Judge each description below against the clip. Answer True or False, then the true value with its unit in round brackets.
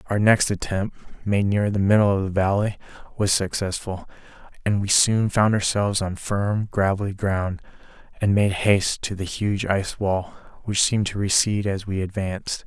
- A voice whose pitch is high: False (100 Hz)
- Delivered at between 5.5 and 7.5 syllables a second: False (4.9 syllables/s)